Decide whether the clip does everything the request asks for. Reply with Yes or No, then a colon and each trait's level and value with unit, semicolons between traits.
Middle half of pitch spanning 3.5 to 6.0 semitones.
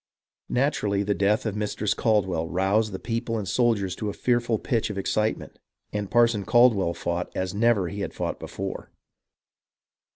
No: average, 3.0 semitones